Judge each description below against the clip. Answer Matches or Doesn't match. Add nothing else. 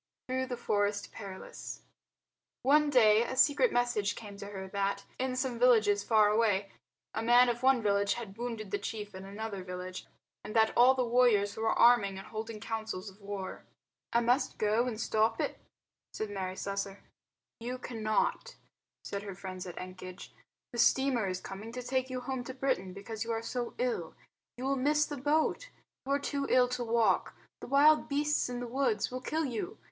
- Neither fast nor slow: Matches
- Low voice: Doesn't match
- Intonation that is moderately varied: Matches